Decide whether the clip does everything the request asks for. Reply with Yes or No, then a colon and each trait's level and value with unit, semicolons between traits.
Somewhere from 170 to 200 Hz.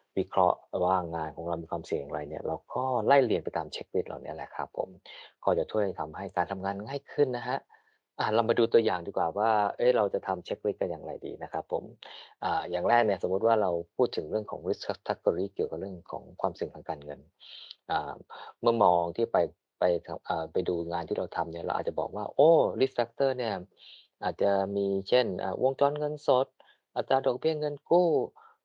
No: low, 120 Hz